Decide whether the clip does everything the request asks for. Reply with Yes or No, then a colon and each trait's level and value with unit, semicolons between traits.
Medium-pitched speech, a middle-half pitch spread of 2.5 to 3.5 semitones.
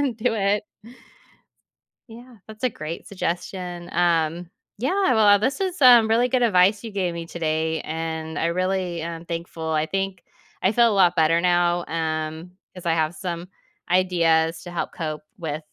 No: medium, 175 Hz; average, 4.0 semitones